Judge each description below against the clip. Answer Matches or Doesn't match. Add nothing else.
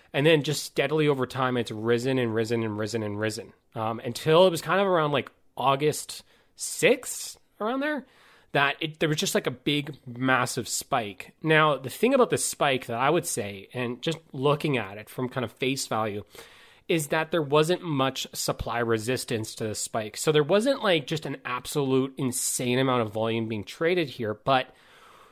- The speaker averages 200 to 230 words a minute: Doesn't match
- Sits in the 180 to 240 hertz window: Doesn't match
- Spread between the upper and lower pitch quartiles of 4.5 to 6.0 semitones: Matches